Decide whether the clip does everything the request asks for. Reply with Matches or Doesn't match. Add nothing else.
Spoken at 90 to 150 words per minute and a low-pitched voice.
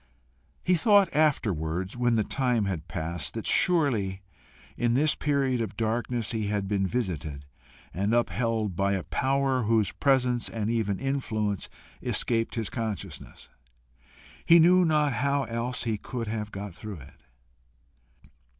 Matches